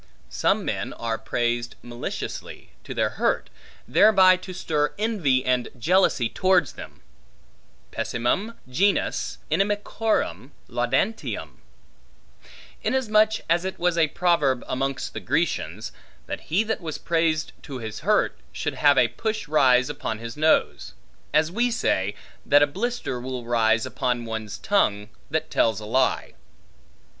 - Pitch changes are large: Yes, wide, 7.8 semitones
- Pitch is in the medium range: Yes, medium, 150 Hz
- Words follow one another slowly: Yes, slow, 130 wpm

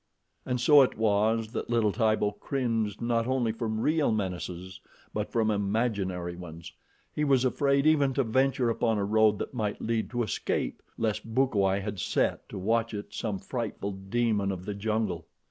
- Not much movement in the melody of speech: No, average, 3.0 semitones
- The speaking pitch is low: Yes, low, 110 Hz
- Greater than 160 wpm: Yes, average, 170 wpm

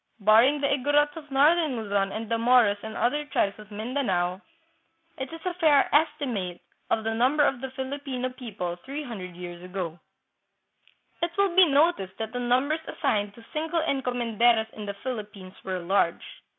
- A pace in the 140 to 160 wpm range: No, average, 170 wpm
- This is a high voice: Yes, high, 245 Hz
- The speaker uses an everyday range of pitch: No, wide, 5.9 semitones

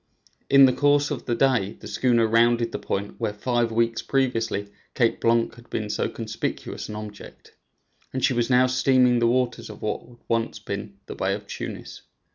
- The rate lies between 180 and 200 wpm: Yes, average, 190 wpm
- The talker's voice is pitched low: Yes, low, 115 Hz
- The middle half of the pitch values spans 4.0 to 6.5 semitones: No, average, 2.9 semitones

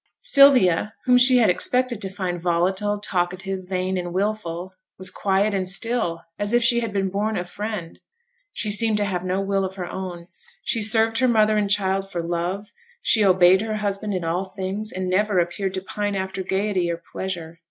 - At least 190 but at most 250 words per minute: Yes, average, 195 wpm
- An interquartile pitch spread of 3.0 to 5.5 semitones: No, narrow, 2.5 semitones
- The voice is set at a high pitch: Yes, high, 195 Hz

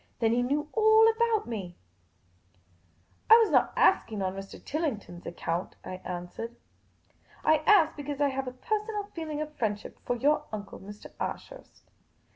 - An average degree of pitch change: No, wide, 9.0 semitones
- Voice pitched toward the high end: Yes, very high, 255 Hz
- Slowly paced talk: No, average, 170 wpm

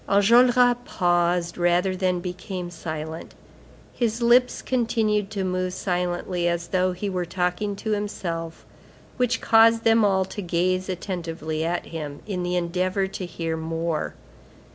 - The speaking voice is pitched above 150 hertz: Yes, medium, 185 Hz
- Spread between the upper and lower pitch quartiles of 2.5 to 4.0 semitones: Yes, average, 3.2 semitones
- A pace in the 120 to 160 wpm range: Yes, average, 140 wpm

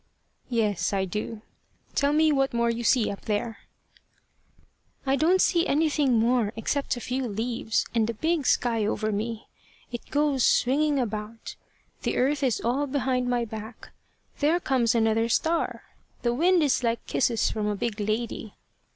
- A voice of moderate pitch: No, high, 240 Hz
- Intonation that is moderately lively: Yes, average, 4.0 semitones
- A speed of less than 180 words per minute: Yes, average, 160 wpm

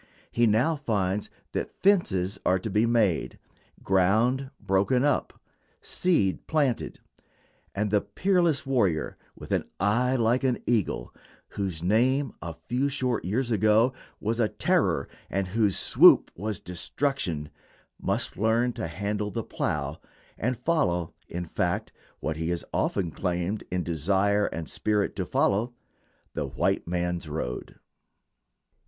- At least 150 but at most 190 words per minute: No, slow, 135 wpm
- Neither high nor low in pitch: No, low, 105 Hz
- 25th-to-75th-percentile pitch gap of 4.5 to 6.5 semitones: Yes, wide, 5.4 semitones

